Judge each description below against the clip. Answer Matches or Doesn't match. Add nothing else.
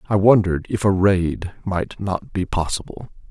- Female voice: Doesn't match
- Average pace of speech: Matches